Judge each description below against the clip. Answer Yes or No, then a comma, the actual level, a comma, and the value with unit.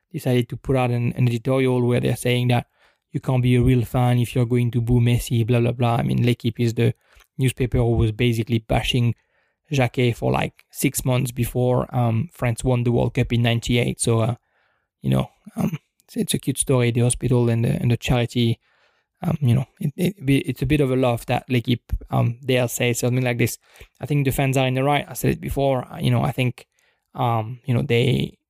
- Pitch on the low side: Yes, low, 125 Hz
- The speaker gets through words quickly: Yes, fast, 225 wpm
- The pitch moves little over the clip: Yes, narrow, 1.6 semitones